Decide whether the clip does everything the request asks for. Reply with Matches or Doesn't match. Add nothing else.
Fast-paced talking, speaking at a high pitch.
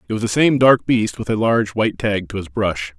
Doesn't match